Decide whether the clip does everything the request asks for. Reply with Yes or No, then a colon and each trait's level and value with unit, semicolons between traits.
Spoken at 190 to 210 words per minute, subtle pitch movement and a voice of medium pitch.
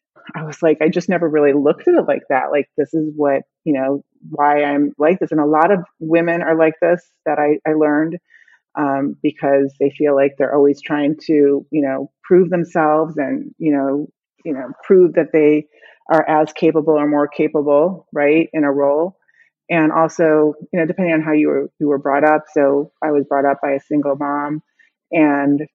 Yes: fast, 205 wpm; narrow, 2.1 semitones; medium, 150 Hz